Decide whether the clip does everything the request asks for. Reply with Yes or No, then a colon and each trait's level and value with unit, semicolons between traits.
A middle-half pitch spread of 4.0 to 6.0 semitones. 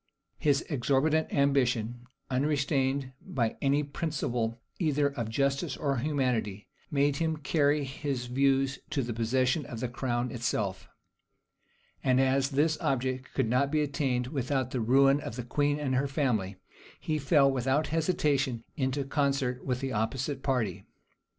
No: narrow, 2.5 semitones